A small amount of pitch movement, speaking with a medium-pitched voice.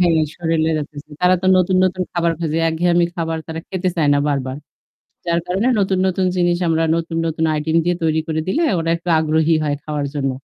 Yes: narrow, 2.0 semitones; medium, 165 Hz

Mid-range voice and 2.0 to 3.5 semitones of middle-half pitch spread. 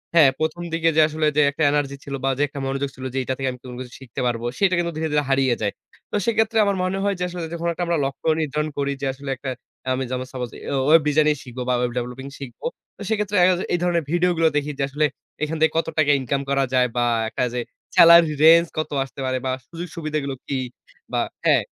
No: medium, 150 Hz; average, 4.0 semitones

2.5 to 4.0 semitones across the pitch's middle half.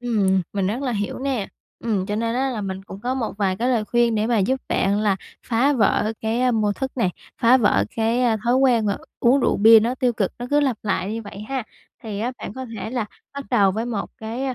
Yes: average, 3.4 semitones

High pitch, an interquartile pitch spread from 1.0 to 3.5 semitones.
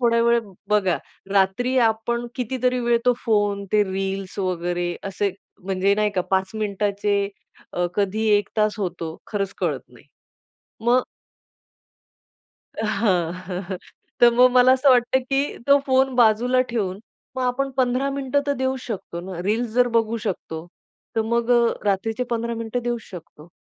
No: high, 220 Hz; average, 4.2 semitones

